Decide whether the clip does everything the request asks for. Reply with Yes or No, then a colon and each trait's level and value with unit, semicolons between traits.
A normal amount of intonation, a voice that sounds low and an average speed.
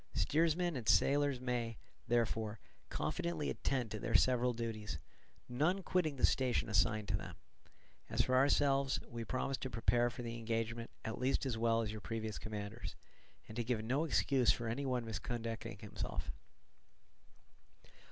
Yes: average, 3.0 semitones; low, 120 Hz; average, 150 wpm